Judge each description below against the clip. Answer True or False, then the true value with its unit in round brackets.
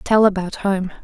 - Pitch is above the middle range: True (195 Hz)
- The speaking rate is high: False (175 wpm)